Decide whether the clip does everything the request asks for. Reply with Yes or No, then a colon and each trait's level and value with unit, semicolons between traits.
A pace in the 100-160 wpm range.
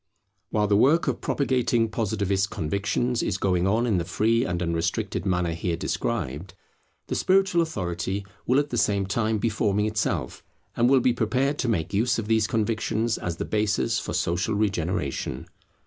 No: average, 170 wpm